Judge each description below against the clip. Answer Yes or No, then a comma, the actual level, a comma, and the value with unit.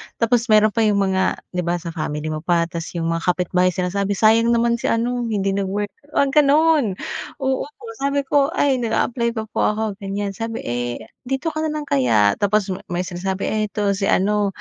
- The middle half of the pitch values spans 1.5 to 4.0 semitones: No, average, 4.5 semitones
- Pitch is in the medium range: No, high, 205 Hz